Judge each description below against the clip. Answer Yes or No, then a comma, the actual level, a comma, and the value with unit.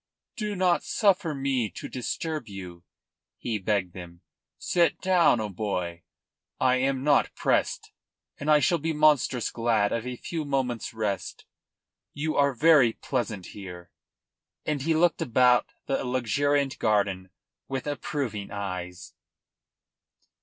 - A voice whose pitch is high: No, low, 125 Hz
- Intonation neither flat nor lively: No, wide, 6.4 semitones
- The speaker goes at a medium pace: No, slow, 125 wpm